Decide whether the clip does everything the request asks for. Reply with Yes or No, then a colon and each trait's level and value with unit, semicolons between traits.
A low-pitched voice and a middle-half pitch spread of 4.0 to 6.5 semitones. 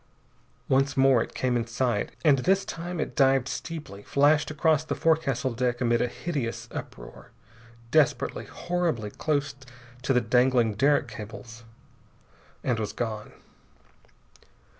Yes: low, 130 Hz; average, 4.3 semitones